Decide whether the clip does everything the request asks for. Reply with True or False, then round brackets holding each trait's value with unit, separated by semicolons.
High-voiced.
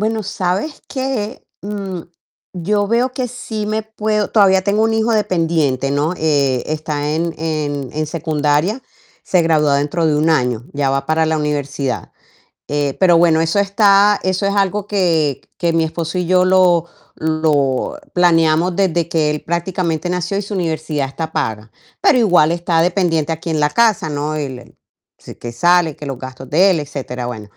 False (165 Hz)